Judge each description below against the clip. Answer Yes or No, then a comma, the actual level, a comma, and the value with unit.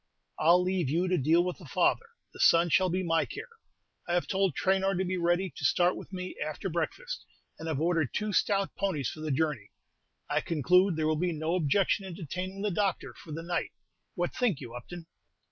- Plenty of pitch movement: No, average, 3.0 semitones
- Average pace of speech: No, fast, 210 wpm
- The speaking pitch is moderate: Yes, medium, 175 Hz